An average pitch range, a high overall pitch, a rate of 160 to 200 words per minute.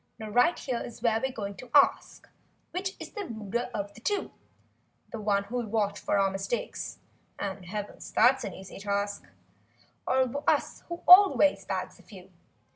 Yes: average, 4.5 semitones; high, 225 Hz; average, 165 wpm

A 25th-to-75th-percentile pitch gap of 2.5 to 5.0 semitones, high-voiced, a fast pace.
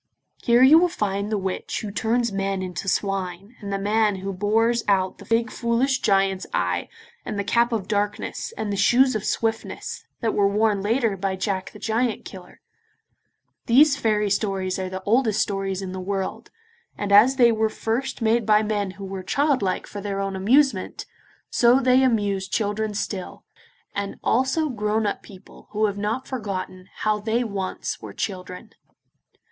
No: average, 3.0 semitones; high, 210 Hz; average, 175 wpm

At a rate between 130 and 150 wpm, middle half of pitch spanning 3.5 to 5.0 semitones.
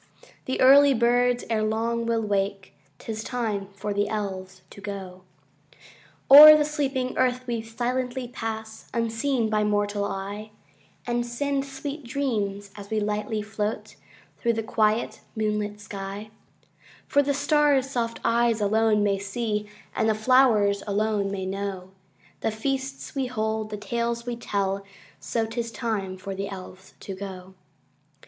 No: average, 145 wpm; average, 3.1 semitones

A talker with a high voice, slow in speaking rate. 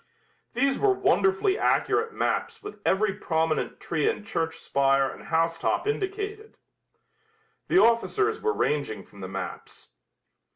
Yes: high, 210 Hz; slow, 130 wpm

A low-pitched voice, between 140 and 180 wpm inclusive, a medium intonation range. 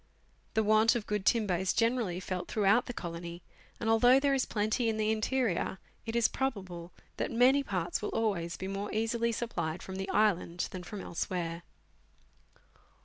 No: high, 210 Hz; average, 175 wpm; average, 4.1 semitones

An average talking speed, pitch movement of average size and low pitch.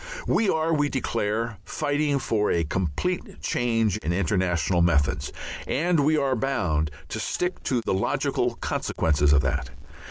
No: average, 145 wpm; wide, 8.8 semitones; low, 110 Hz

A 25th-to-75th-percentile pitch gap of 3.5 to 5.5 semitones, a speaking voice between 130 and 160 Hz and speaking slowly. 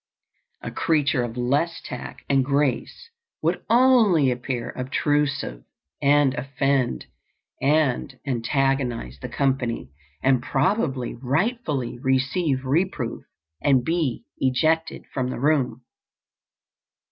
No: average, 3.0 semitones; low, 135 Hz; slow, 100 wpm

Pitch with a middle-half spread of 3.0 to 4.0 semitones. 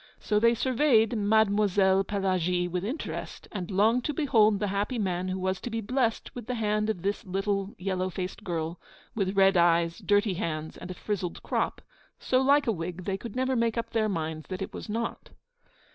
Yes: average, 3.4 semitones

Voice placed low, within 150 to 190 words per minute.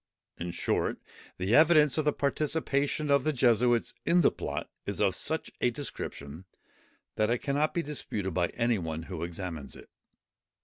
Yes: low, 120 Hz; average, 165 wpm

